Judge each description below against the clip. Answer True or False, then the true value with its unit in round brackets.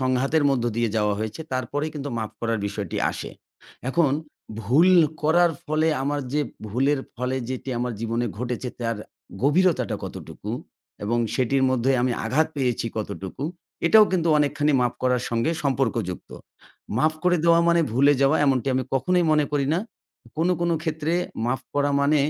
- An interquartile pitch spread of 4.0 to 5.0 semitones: True (4.3 semitones)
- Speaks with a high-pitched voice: False (135 Hz)